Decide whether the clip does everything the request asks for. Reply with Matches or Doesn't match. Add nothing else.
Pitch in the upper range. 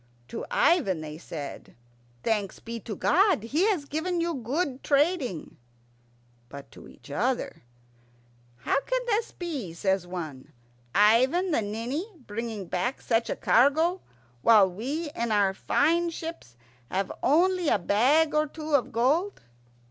Matches